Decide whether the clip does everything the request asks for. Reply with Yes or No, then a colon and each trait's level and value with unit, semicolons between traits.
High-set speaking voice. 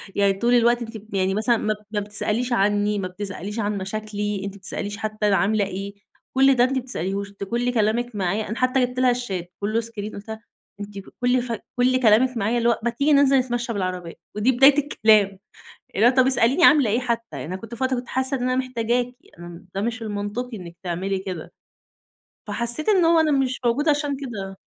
Yes: high, 225 Hz